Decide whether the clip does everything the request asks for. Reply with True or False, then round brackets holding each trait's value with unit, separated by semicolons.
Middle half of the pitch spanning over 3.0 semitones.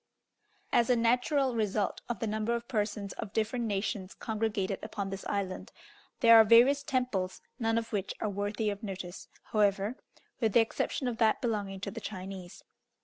False (2.7 semitones)